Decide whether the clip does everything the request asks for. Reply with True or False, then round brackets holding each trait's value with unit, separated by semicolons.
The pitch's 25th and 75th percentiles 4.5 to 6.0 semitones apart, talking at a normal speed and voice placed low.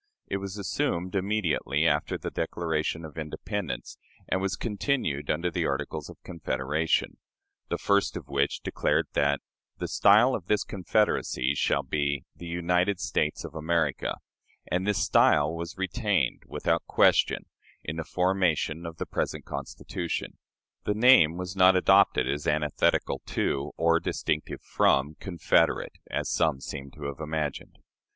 False (4.1 semitones; 145 wpm; 85 Hz)